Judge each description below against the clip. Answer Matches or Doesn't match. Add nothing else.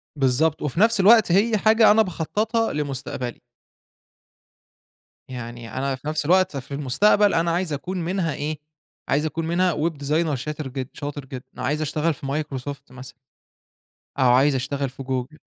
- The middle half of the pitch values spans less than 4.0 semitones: Doesn't match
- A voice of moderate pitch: Matches